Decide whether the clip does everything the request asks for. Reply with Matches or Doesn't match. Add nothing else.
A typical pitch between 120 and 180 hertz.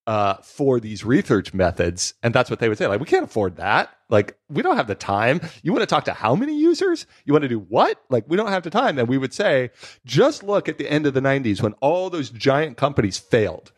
Matches